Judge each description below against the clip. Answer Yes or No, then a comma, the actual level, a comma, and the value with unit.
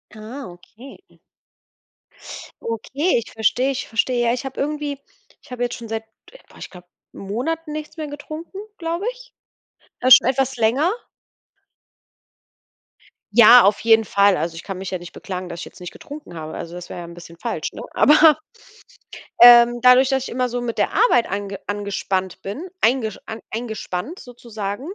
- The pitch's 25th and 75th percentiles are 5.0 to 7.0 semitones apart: Yes, average, 5.3 semitones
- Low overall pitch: No, high, 235 Hz